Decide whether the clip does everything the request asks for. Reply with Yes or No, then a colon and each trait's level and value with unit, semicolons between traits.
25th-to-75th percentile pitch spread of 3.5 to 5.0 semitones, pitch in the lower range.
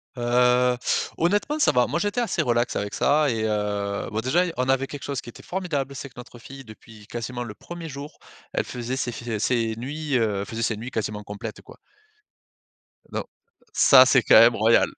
Yes: average, 3.9 semitones; low, 125 Hz